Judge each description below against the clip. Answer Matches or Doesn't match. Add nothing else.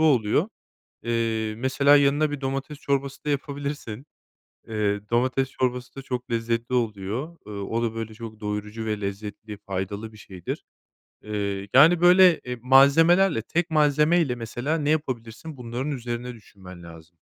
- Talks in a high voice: Doesn't match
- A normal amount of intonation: Matches